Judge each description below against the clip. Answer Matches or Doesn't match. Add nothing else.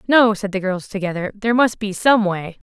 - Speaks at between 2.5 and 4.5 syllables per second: Doesn't match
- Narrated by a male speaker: Doesn't match